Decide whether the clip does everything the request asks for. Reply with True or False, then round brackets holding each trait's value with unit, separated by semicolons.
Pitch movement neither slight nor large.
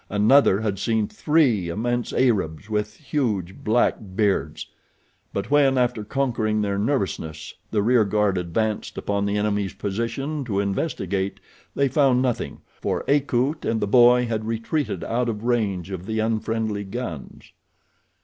True (3.5 semitones)